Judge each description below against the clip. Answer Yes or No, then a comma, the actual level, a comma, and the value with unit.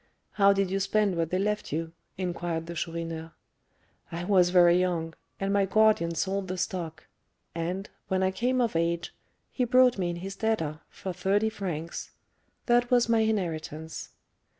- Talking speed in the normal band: Yes, average, 165 wpm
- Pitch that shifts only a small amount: No, average, 3.6 semitones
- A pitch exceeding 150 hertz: Yes, medium, 185 Hz